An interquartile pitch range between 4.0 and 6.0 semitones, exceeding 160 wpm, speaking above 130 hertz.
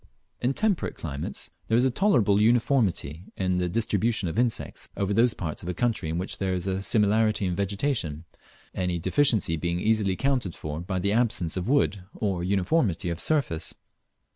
No: average, 4.7 semitones; average, 180 wpm; low, 100 Hz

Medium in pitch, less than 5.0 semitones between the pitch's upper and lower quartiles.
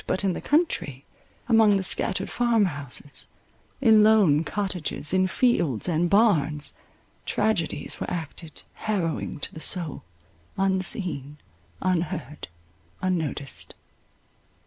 No: medium, 180 Hz; average, 5.3 semitones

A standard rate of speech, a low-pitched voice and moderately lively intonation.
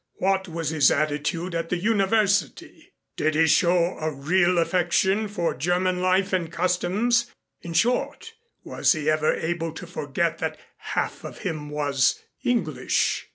No: average, 145 wpm; medium, 175 Hz; average, 3.3 semitones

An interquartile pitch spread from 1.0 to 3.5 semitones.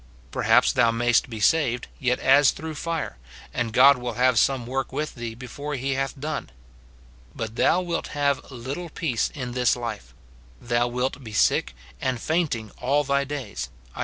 Yes: average, 3.2 semitones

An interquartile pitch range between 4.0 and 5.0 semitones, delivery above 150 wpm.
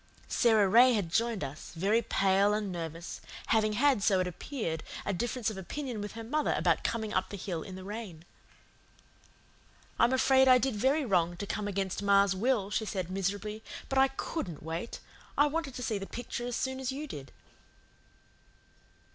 Yes: average, 4.6 semitones; average, 180 wpm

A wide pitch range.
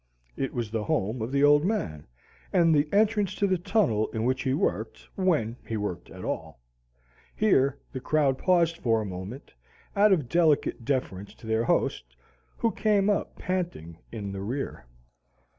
Yes: wide, 8.4 semitones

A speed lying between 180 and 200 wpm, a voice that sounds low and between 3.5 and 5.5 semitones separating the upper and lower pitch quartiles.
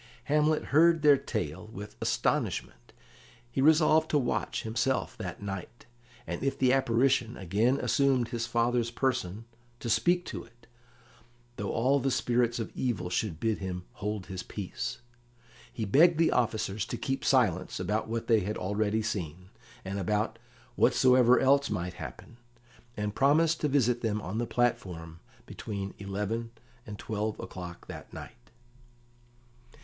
No: average, 145 wpm; low, 115 Hz; average, 4.8 semitones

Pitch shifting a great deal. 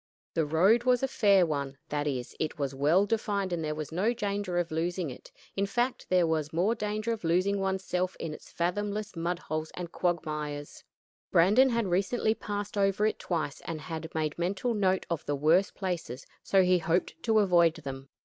No: average, 4.3 semitones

